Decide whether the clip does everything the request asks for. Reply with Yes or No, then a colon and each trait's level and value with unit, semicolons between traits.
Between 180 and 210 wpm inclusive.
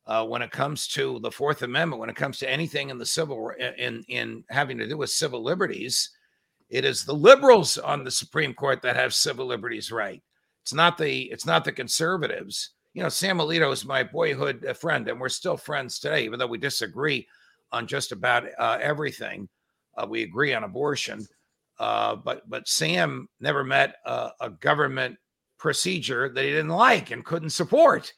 Yes: average, 185 wpm